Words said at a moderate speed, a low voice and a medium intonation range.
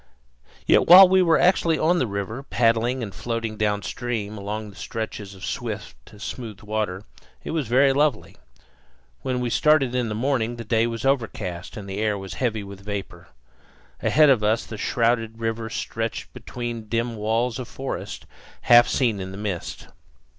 Yes: average, 170 wpm; low, 115 Hz; average, 3.1 semitones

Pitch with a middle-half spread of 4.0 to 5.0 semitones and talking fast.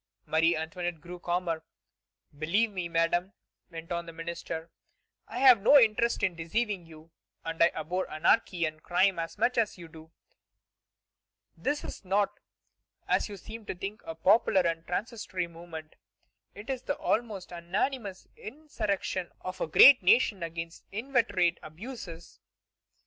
No: average, 4.3 semitones; average, 145 wpm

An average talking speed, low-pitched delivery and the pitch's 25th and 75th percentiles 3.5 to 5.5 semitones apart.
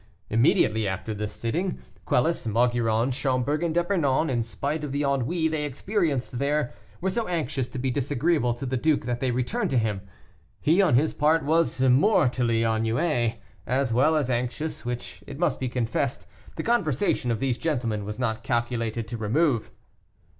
Yes: average, 170 wpm; low, 130 Hz; average, 4.5 semitones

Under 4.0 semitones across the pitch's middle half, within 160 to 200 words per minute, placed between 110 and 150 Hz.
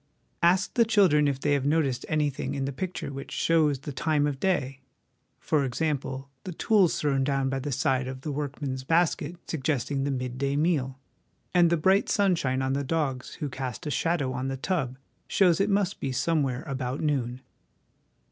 Yes: average, 3.6 semitones; average, 185 wpm; medium, 140 Hz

